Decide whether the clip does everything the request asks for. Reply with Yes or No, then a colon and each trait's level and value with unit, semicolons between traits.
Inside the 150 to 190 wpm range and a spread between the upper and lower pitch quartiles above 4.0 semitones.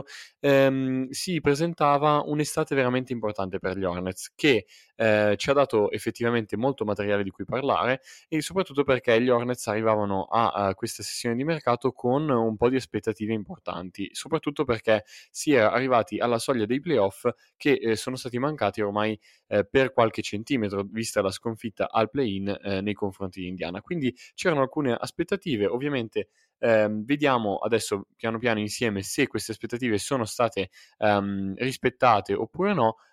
Yes: average, 160 wpm; average, 4.5 semitones